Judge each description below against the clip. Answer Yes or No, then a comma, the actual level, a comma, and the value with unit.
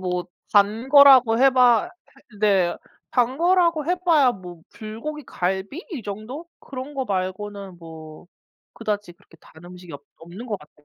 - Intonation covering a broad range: Yes, wide, 6.8 semitones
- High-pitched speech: Yes, high, 215 Hz